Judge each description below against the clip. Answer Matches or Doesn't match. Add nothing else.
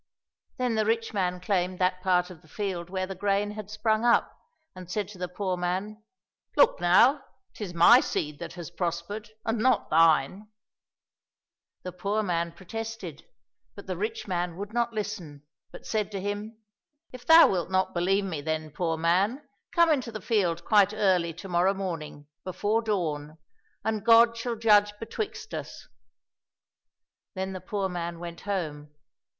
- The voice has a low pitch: Doesn't match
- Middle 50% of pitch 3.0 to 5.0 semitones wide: Matches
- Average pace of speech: Matches